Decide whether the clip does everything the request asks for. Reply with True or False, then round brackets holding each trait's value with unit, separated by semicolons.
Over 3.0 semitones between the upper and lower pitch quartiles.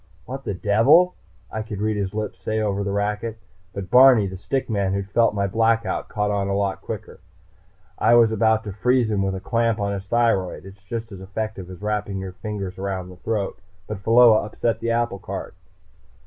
False (2.5 semitones)